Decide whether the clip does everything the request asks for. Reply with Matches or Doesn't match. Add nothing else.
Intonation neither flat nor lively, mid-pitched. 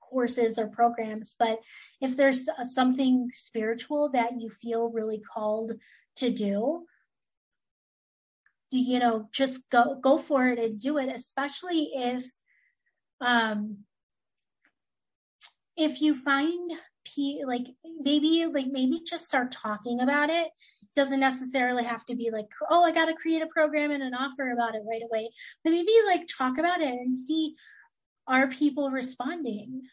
Doesn't match